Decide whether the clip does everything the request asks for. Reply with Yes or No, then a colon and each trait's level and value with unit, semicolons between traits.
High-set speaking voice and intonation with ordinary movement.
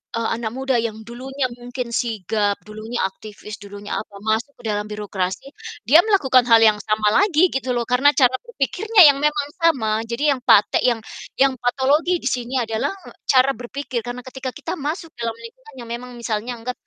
Yes: high, 245 Hz; average, 3.7 semitones